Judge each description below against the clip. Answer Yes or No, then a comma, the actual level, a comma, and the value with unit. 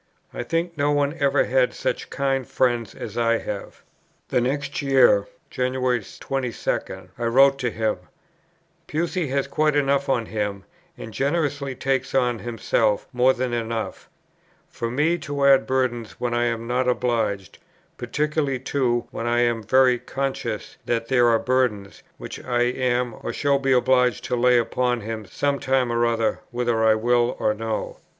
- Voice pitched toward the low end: Yes, low, 125 Hz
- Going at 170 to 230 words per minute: No, average, 160 wpm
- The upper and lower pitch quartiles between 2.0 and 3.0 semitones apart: Yes, average, 2.7 semitones